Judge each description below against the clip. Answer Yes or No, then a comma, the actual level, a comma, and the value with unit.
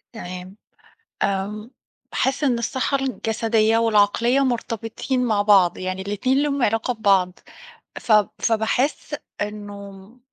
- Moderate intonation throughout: Yes, average, 3.5 semitones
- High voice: Yes, high, 220 Hz